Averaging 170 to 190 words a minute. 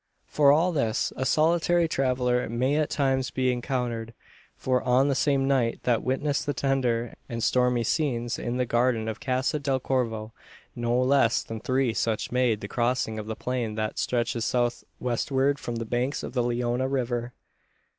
Yes: average, 175 wpm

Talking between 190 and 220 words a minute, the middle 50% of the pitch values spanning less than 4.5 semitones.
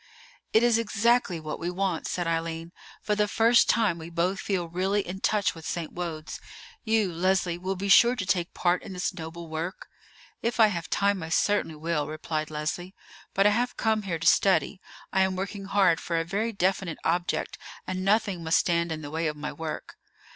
Yes: average, 200 wpm; average, 3.4 semitones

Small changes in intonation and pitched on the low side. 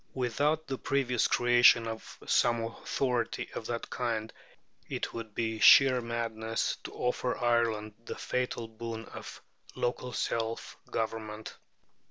Yes: narrow, 1.7 semitones; low, 115 Hz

